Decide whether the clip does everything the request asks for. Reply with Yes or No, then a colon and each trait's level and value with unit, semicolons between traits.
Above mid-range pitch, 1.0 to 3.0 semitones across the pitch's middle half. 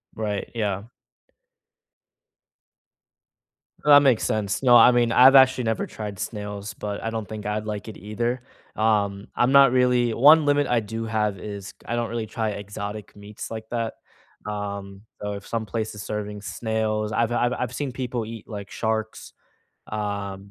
No: low, 110 Hz; narrow, 2.5 semitones